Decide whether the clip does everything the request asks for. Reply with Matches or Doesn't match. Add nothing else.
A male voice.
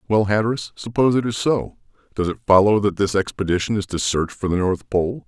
Matches